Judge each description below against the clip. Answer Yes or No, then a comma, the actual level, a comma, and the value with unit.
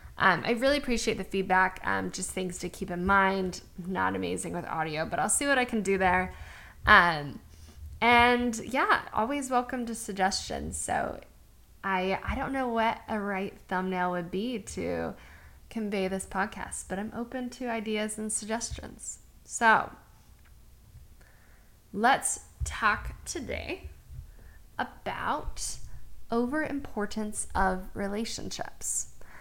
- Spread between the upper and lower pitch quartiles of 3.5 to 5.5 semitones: Yes, average, 4.4 semitones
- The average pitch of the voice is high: Yes, high, 195 Hz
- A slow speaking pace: Yes, slow, 130 wpm